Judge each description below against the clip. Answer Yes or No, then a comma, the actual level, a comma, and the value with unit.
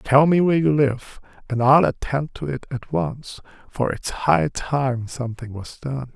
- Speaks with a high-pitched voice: No, low, 130 Hz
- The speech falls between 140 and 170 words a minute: No, average, 185 wpm